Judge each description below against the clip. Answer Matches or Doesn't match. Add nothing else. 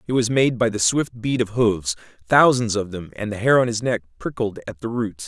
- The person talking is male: Matches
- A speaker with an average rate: Doesn't match